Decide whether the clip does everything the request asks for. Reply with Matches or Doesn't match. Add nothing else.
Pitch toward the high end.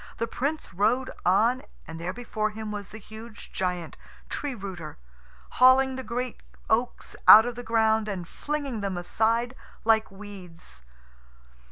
Matches